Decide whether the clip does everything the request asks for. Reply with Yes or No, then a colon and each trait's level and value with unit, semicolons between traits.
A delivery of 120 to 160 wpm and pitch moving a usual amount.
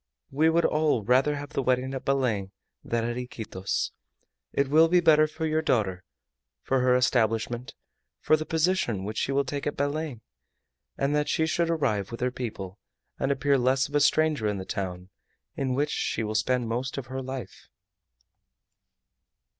No: average, 170 wpm; average, 4.3 semitones